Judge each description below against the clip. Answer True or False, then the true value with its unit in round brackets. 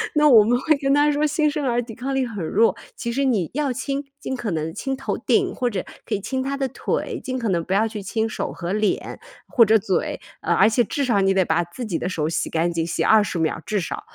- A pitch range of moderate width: False (5.9 semitones)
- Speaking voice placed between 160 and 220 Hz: False (230 Hz)